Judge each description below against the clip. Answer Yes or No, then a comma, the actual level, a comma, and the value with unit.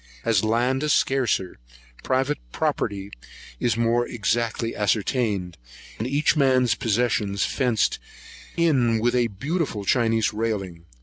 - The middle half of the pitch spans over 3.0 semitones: Yes, average, 3.5 semitones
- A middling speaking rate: No, slow, 115 wpm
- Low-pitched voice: Yes, low, 115 Hz